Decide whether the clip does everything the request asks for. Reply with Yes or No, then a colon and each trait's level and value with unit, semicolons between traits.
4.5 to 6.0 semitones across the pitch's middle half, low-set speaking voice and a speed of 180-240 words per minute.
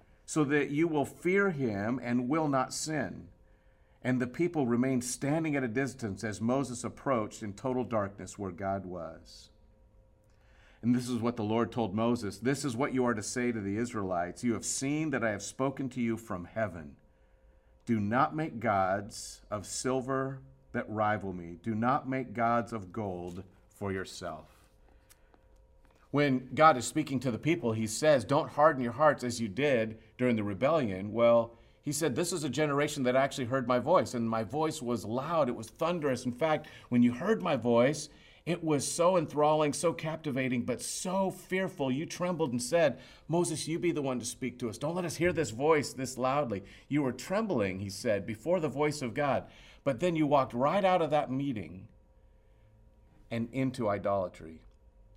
Yes: wide, 5.6 semitones; low, 125 Hz; average, 185 wpm